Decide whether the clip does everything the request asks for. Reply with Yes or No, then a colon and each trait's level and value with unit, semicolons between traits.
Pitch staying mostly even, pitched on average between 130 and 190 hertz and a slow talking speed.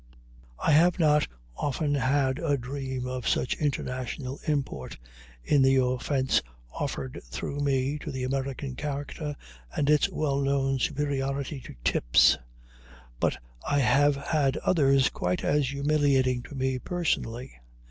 Yes: narrow, 1.9 semitones; low, 135 Hz; slow, 130 wpm